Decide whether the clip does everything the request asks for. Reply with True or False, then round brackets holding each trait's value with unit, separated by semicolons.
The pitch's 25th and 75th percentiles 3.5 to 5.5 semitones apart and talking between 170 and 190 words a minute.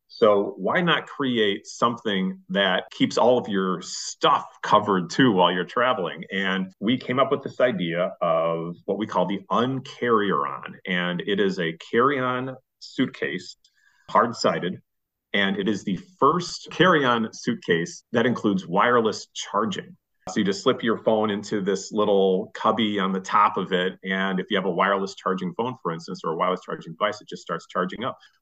True (4.4 semitones; 180 wpm)